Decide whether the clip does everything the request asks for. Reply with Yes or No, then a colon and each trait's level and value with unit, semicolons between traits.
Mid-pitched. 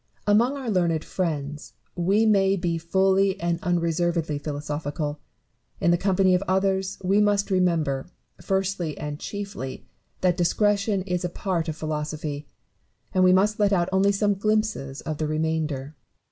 Yes: medium, 180 Hz